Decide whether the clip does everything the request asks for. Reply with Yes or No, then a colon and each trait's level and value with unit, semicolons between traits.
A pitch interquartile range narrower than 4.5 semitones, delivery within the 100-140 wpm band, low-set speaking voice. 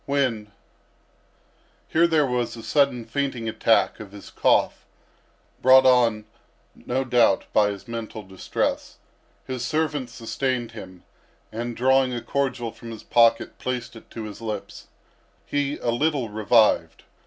Yes: average, 2.9 semitones; slow, 135 wpm; low, 120 Hz